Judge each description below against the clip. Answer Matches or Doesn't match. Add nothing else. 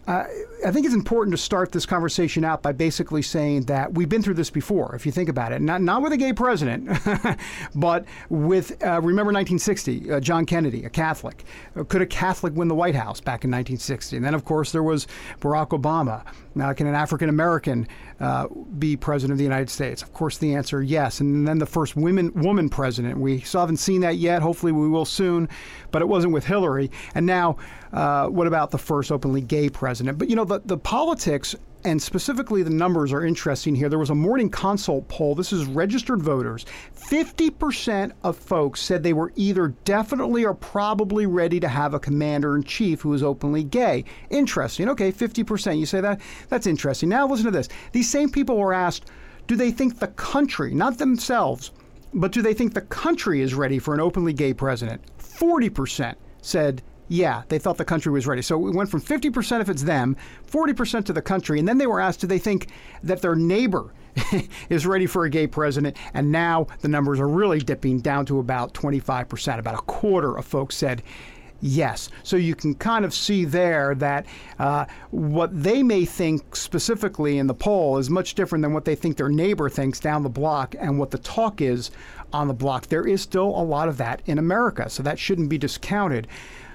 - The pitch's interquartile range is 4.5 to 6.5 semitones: Matches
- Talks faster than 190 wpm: Matches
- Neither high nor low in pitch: Matches